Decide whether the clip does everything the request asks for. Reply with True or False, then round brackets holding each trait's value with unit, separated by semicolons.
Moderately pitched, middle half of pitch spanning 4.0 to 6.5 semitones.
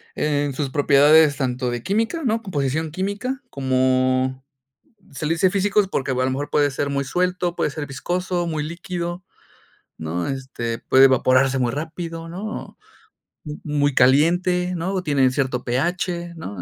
True (150 Hz; 5.2 semitones)